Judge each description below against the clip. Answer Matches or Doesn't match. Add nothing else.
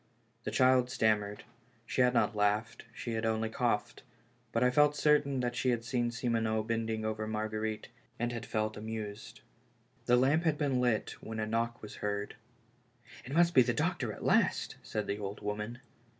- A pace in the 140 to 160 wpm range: Doesn't match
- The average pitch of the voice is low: Matches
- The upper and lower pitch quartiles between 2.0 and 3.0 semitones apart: Matches